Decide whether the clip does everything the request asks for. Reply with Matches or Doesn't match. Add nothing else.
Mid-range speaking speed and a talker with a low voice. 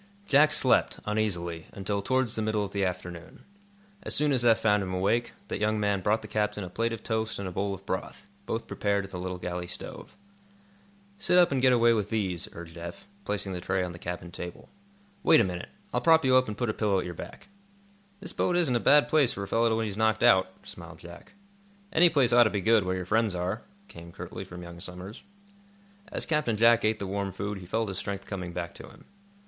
Doesn't match